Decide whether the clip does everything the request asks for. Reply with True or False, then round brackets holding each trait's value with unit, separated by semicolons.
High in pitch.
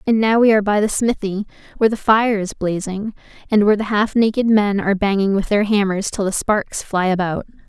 True (205 Hz)